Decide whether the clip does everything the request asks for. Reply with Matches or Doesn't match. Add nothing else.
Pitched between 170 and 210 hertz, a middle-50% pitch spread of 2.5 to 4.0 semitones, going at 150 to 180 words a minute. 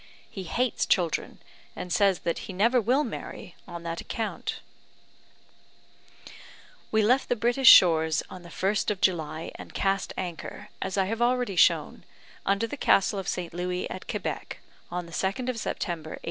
Doesn't match